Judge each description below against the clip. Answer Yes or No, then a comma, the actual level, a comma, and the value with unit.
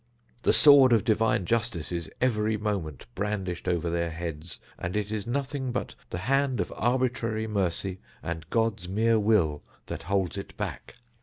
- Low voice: Yes, low, 105 Hz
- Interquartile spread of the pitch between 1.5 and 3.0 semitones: No, average, 4.8 semitones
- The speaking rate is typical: Yes, average, 160 wpm